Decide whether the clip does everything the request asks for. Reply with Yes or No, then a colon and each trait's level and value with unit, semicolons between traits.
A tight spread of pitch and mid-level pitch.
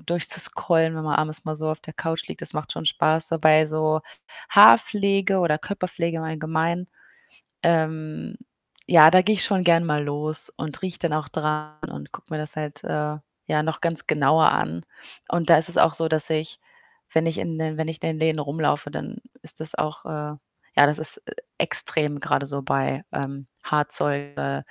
Yes: narrow, 1.5 semitones; medium, 155 Hz